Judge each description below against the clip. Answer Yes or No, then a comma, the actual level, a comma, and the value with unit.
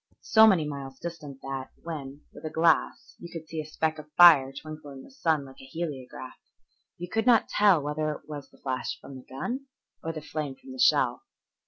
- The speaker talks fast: Yes, fast, 210 wpm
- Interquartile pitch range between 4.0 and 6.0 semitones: No, average, 3.6 semitones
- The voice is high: No, medium, 155 Hz